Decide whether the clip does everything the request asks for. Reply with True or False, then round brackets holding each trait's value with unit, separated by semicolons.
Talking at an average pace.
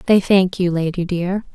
True (195 wpm)